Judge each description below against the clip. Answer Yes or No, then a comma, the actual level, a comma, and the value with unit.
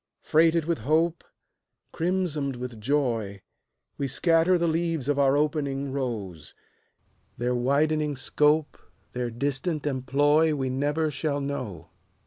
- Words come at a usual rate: No, slow, 115 wpm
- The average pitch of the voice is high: No, medium, 145 Hz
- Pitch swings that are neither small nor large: Yes, average, 3.4 semitones